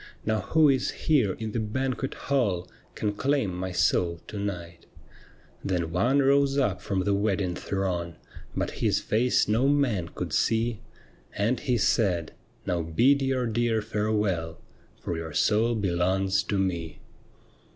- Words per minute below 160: Yes, average, 150 wpm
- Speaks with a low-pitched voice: Yes, low, 105 Hz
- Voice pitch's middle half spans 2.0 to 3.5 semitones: No, average, 5.1 semitones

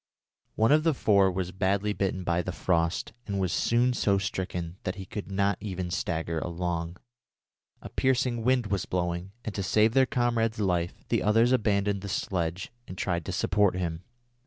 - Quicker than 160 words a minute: Yes, average, 180 wpm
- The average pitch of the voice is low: Yes, very low, 95 Hz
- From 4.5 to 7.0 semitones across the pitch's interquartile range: No, average, 3.4 semitones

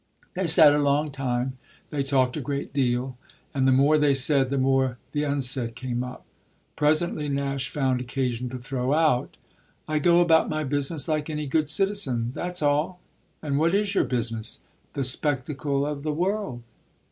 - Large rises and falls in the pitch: No, average, 3.0 semitones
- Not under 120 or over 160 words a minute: No, average, 170 wpm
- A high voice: No, medium, 140 Hz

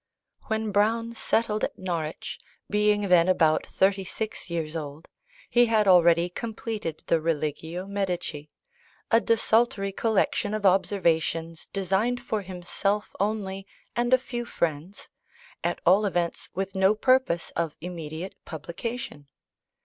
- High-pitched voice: Yes, high, 195 Hz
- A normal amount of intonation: Yes, average, 4.2 semitones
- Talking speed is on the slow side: Yes, slow, 125 wpm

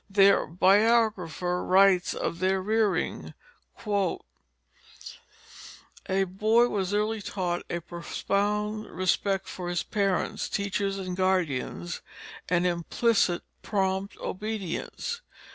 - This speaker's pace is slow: Yes, slow, 95 wpm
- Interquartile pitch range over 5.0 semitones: No, narrow, 2.6 semitones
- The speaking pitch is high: Yes, high, 195 Hz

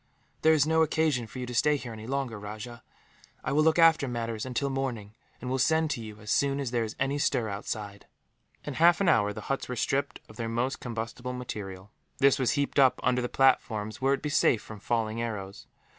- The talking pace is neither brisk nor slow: No, fast, 225 wpm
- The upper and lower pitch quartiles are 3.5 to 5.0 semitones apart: Yes, average, 3.9 semitones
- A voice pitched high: No, low, 125 Hz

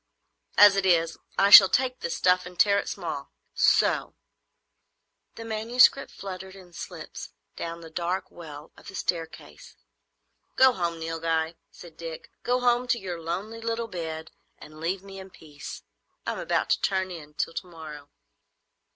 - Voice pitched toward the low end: No, medium, 180 Hz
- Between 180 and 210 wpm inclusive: No, average, 160 wpm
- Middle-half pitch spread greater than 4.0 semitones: No, average, 3.6 semitones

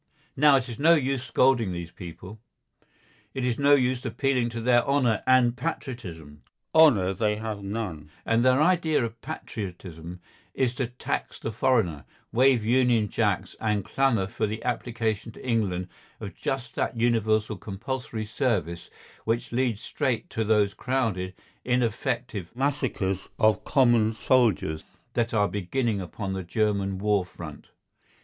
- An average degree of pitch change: Yes, average, 4.3 semitones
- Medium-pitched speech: No, low, 115 Hz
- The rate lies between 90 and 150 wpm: Yes, average, 140 wpm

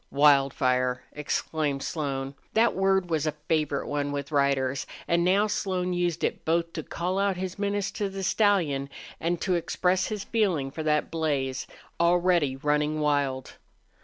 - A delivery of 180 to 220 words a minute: No, average, 155 wpm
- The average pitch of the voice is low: No, medium, 160 Hz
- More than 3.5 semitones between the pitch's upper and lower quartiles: Yes, average, 4.6 semitones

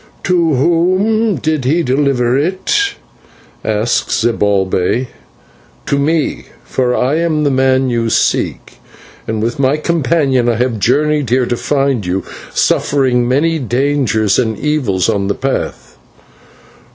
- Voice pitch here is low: Yes, low, 130 Hz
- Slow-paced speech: Yes, slow, 125 wpm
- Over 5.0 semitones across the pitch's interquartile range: No, average, 4.3 semitones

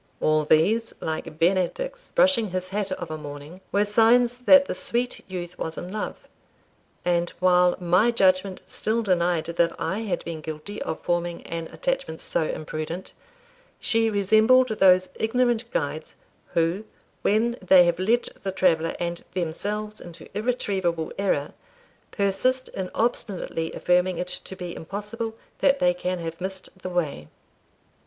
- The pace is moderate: Yes, average, 145 wpm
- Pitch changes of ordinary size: Yes, average, 4.4 semitones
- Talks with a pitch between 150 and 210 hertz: Yes, medium, 185 Hz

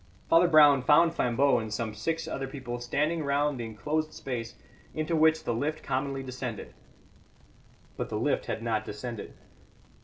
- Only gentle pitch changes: No, average, 4.7 semitones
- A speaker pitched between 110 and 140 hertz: Yes, low, 135 Hz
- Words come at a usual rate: Yes, average, 155 wpm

